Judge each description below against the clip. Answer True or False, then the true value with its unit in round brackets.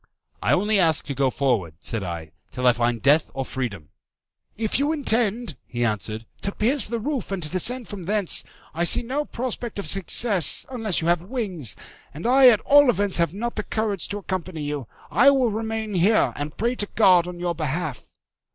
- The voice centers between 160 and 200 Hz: True (190 Hz)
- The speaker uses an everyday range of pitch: False (7.6 semitones)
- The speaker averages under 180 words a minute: False (195 wpm)